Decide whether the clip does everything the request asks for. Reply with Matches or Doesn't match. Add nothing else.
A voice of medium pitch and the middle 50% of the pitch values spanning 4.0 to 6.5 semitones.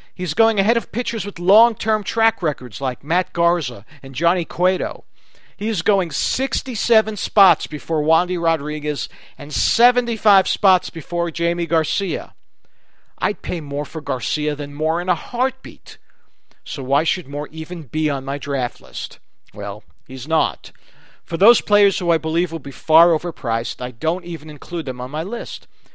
Matches